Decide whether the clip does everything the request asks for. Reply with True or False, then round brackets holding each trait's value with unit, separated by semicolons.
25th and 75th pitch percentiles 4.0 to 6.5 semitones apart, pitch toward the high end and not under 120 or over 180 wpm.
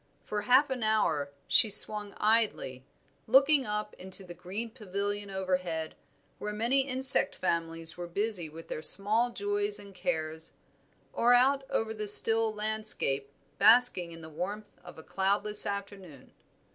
True (4.3 semitones; 205 Hz; 145 wpm)